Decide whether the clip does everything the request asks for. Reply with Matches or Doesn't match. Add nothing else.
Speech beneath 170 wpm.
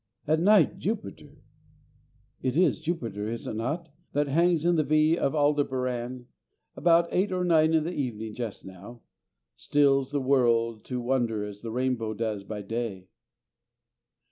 Matches